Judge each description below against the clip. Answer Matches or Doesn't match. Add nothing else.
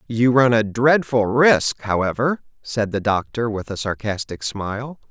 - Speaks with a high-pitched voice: Doesn't match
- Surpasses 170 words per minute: Doesn't match